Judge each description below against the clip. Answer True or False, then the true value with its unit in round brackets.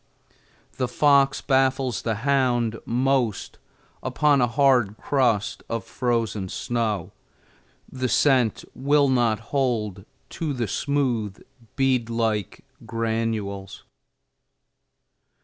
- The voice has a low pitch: True (120 Hz)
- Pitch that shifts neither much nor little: True (3.2 semitones)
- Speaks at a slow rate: True (95 wpm)